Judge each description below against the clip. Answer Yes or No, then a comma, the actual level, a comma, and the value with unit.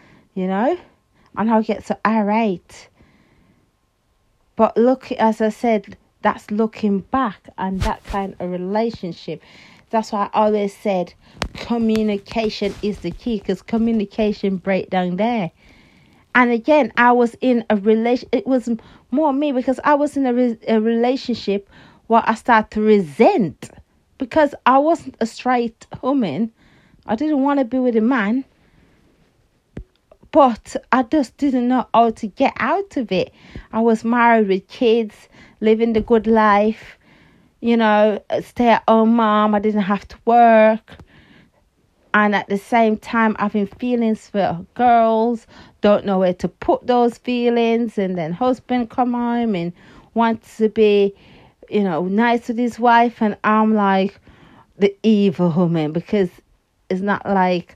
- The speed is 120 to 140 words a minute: No, average, 150 wpm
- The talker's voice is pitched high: Yes, high, 220 Hz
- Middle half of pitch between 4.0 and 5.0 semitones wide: No, average, 3.0 semitones